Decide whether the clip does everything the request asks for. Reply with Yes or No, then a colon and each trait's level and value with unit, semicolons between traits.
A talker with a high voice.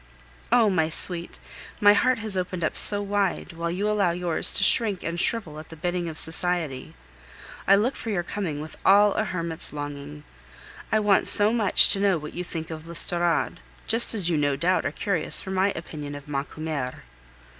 No: medium, 175 Hz